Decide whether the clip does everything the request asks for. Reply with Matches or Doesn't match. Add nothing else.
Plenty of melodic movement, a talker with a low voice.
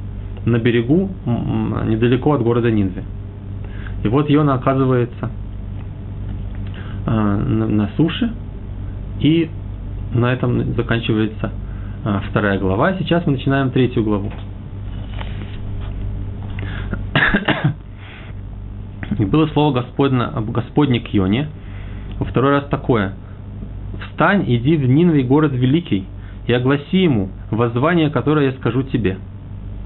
Doesn't match